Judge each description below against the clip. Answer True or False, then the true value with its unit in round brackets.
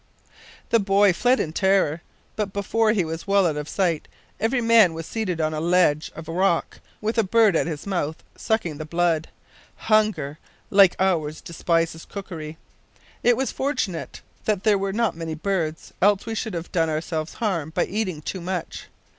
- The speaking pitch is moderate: True (180 Hz)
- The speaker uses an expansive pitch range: False (4.4 semitones)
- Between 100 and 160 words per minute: False (175 wpm)